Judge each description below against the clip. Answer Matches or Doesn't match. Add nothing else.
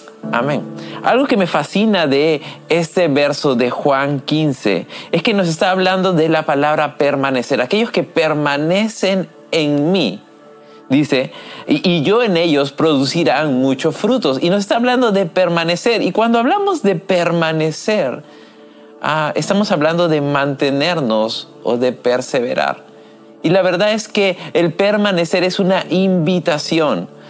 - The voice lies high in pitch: Doesn't match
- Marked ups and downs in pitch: Doesn't match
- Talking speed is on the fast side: Doesn't match